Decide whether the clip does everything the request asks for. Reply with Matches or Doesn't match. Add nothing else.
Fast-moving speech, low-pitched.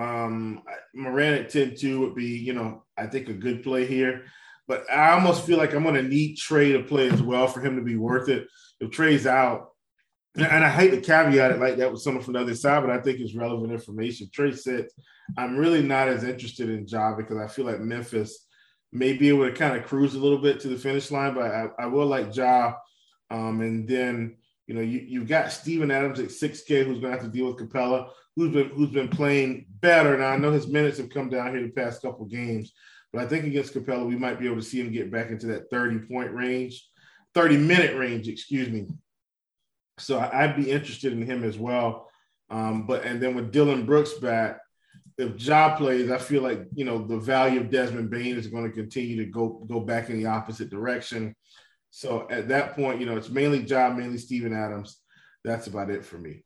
Matches